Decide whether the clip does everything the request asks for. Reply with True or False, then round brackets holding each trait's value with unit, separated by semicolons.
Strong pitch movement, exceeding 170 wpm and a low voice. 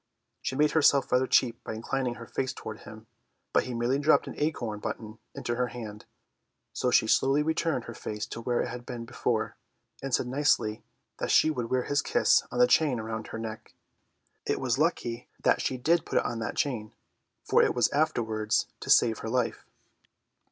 False (3.5 semitones; 195 wpm; 125 Hz)